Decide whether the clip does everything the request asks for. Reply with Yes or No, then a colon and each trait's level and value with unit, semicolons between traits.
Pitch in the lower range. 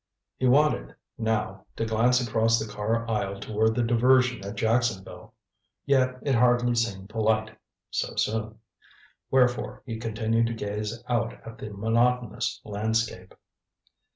Yes: low, 115 Hz